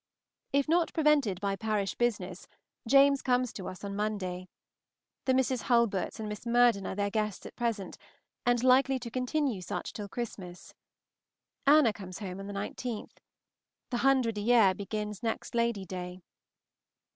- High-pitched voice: Yes, high, 220 Hz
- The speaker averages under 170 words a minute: Yes, average, 155 wpm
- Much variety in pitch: No, average, 4.1 semitones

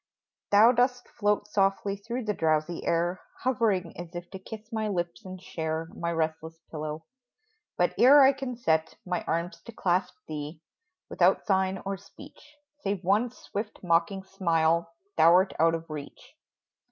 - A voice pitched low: No, medium, 185 Hz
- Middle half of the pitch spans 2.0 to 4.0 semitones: No, average, 4.4 semitones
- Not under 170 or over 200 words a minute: No, average, 155 wpm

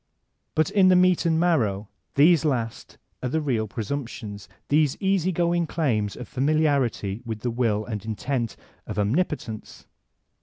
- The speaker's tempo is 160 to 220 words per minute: No, average, 150 wpm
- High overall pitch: No, low, 135 Hz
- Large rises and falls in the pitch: Yes, wide, 6.6 semitones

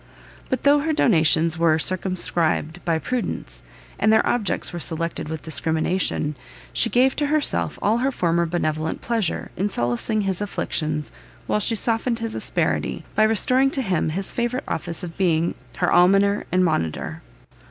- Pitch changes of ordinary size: No, wide, 6.0 semitones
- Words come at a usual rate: Yes, average, 155 wpm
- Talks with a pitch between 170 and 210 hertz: Yes, medium, 185 Hz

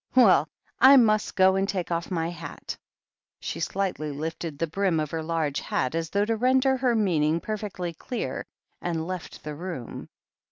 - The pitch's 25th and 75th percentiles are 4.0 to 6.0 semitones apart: Yes, average, 4.6 semitones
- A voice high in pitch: No, medium, 175 Hz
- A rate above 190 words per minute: No, average, 170 wpm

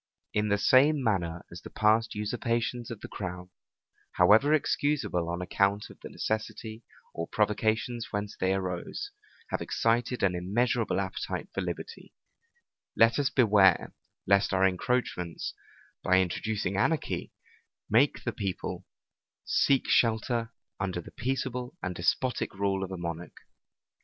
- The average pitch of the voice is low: Yes, low, 105 Hz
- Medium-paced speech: No, slow, 130 wpm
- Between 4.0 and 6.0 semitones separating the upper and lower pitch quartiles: Yes, average, 4.3 semitones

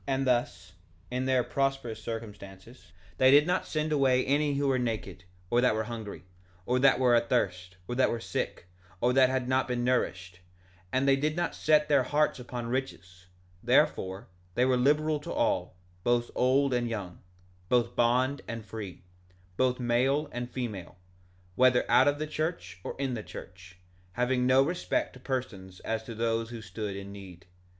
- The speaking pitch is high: No, low, 125 Hz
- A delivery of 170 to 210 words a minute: Yes, average, 175 wpm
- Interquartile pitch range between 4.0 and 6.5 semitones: No, average, 3.6 semitones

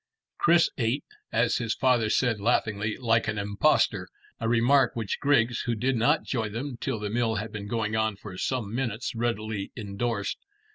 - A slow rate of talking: No, average, 175 wpm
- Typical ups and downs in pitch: No, narrow, 2.3 semitones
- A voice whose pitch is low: Yes, low, 115 Hz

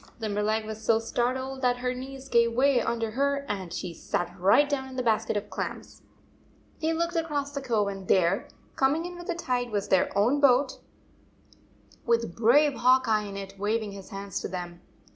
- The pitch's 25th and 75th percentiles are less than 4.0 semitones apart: No, average, 4.8 semitones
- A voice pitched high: Yes, high, 235 Hz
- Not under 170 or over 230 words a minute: Yes, average, 190 wpm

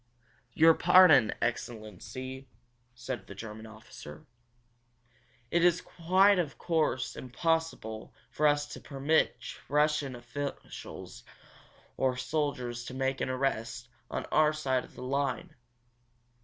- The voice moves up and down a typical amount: Yes, average, 4.2 semitones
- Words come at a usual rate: No, slow, 115 wpm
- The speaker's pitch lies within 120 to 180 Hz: Yes, low, 135 Hz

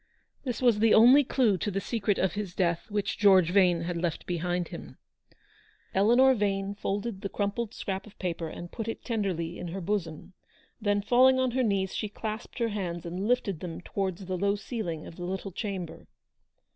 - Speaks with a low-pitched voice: No, high, 200 Hz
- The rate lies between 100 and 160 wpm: No, average, 190 wpm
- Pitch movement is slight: No, average, 3.5 semitones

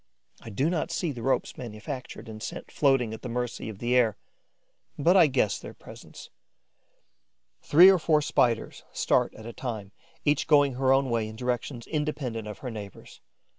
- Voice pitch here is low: Yes, low, 125 Hz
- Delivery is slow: No, average, 175 wpm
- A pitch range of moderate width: Yes, average, 4.3 semitones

